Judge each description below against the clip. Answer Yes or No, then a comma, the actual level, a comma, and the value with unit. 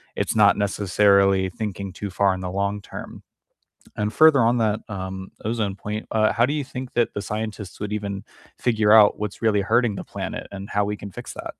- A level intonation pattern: Yes, narrow, 2.0 semitones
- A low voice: Yes, low, 105 Hz